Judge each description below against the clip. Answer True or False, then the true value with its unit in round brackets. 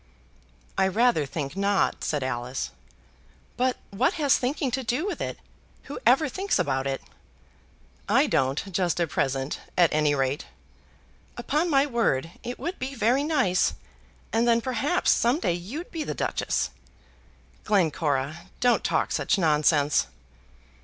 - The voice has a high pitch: True (195 Hz)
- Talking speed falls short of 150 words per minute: True (140 wpm)